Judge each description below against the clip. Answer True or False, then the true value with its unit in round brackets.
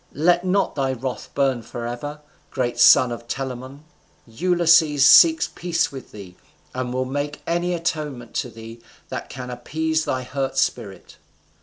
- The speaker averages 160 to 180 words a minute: False (145 wpm)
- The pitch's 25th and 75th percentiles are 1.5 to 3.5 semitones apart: False (4.6 semitones)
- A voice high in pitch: False (135 Hz)